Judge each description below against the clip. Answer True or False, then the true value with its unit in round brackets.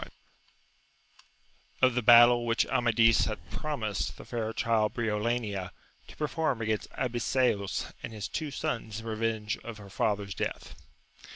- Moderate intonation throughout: False (2.3 semitones)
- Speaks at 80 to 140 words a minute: True (135 wpm)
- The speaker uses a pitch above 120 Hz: False (115 Hz)